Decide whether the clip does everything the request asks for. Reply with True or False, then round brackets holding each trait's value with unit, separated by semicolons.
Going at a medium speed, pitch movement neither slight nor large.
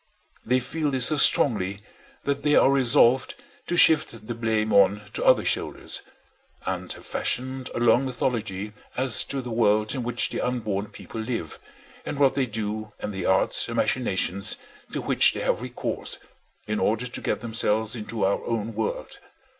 True (170 wpm; 3.3 semitones)